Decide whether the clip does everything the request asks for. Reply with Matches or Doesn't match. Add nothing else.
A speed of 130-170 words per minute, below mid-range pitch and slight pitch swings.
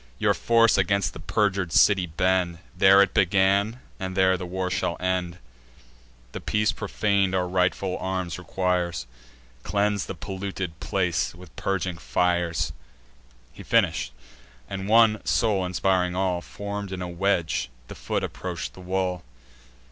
Matches